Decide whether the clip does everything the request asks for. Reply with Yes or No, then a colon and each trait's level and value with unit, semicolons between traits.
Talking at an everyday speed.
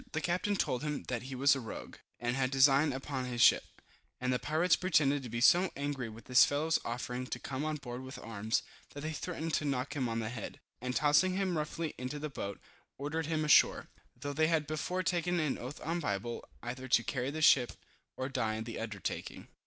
No: fast, 225 wpm